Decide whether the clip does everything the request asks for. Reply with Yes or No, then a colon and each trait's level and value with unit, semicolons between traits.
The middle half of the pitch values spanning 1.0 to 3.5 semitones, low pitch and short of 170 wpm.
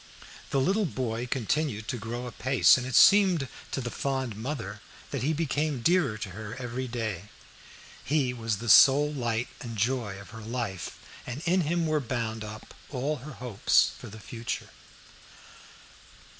No: average, 4.3 semitones; low, 125 Hz; average, 160 wpm